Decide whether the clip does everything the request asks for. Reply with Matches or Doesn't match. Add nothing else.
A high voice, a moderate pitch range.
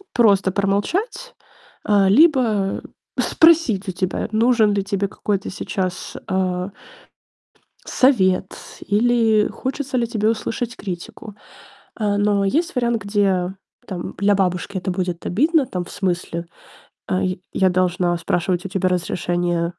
Matches